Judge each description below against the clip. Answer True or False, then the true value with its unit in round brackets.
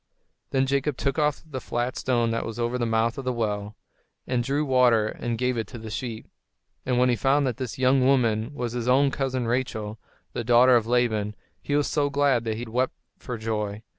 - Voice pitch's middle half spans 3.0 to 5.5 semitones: False (2.5 semitones)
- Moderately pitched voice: False (125 Hz)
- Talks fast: True (215 wpm)